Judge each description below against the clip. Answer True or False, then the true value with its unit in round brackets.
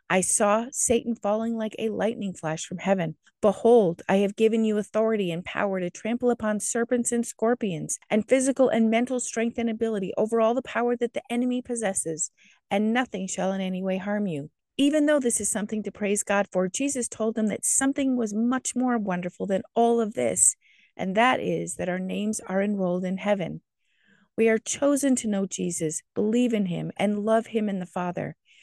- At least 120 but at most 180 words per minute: False (195 wpm)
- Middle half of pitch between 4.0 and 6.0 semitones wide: False (3.4 semitones)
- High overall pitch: True (215 Hz)